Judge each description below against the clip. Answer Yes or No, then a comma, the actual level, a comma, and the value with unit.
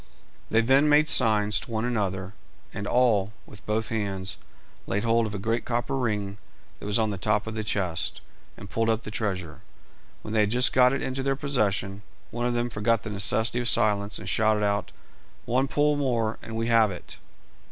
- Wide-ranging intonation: No, average, 2.8 semitones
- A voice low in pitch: Yes, low, 110 Hz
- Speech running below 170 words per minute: No, average, 200 wpm